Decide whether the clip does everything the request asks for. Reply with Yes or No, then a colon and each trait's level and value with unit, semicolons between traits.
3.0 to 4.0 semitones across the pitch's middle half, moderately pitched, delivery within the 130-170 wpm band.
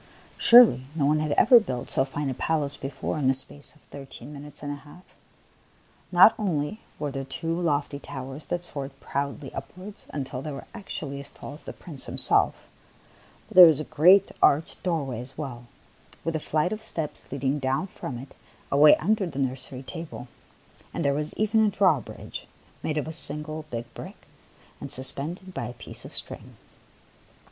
No: average, 3.5 semitones; medium, 145 Hz; average, 185 wpm